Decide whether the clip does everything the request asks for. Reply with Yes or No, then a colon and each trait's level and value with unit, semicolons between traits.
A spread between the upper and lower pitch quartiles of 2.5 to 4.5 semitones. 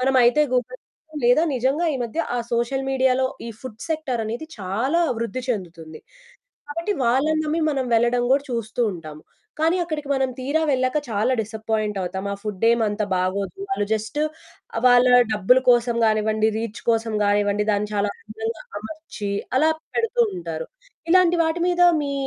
No: average, 5.1 semitones